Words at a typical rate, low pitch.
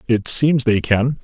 Yes: average, 195 wpm; low, 125 Hz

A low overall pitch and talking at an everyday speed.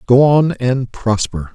Yes: low, 125 Hz; average, 155 wpm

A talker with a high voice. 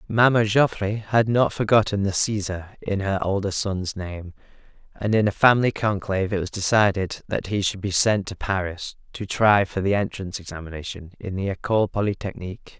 No: low, 100 Hz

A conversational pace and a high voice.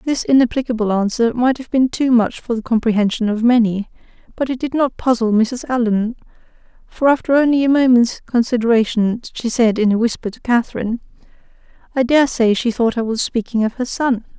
Yes: average, 185 wpm; high, 240 Hz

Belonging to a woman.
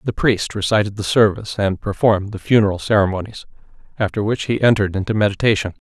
No: male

